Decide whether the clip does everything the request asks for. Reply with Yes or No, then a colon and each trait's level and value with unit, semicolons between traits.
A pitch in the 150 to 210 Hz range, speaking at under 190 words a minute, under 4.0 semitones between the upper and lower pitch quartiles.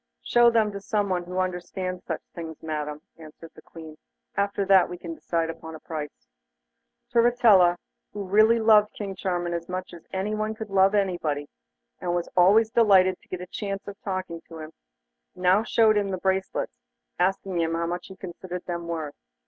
Yes: medium, 185 Hz; average, 175 wpm; average, 3.0 semitones